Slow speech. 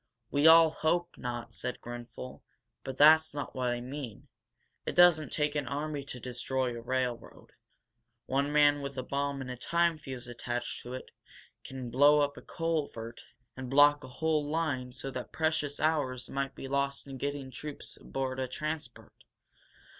No: average, 170 wpm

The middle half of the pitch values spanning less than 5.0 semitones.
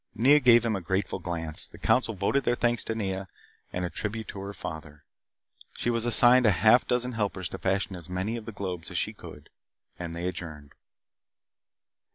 Yes: average, 4.6 semitones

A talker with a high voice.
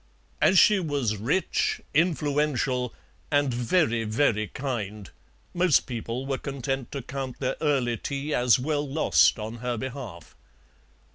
No: low, 130 Hz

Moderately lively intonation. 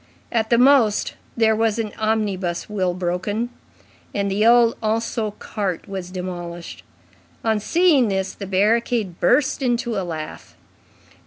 Yes: average, 3.6 semitones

